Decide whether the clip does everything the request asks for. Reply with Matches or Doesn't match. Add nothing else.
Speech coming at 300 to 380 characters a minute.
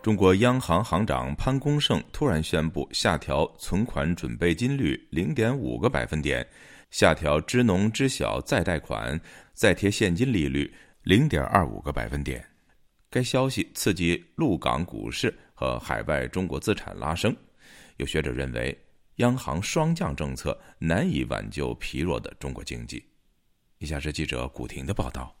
Doesn't match